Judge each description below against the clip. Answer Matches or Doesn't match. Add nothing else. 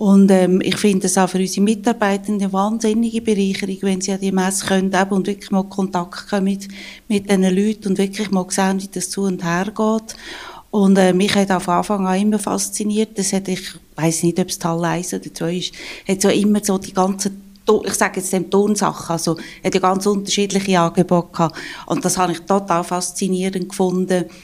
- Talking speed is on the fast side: Matches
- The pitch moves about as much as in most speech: Doesn't match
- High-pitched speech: Matches